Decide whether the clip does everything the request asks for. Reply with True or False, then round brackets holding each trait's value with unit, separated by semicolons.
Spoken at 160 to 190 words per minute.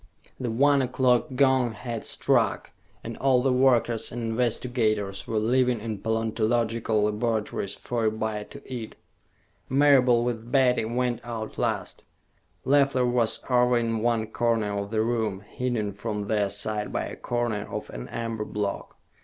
False (150 wpm)